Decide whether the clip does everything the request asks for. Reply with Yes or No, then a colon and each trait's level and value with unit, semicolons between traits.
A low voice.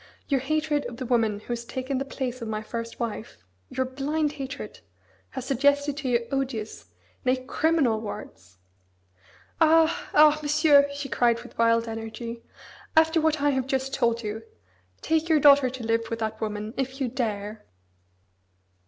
No: very high, 260 Hz